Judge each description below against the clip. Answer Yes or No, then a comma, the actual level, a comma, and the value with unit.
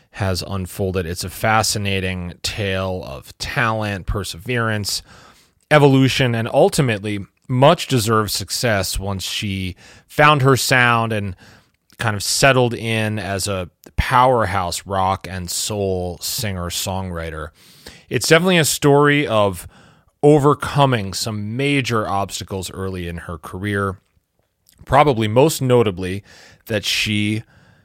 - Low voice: Yes, low, 105 Hz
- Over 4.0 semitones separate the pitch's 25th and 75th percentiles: Yes, average, 4.5 semitones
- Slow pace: Yes, slow, 110 wpm